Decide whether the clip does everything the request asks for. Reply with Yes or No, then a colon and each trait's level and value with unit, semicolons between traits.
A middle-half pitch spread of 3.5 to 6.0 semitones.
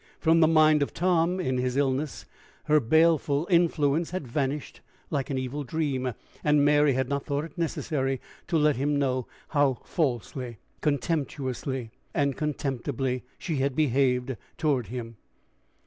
No: average, 2.9 semitones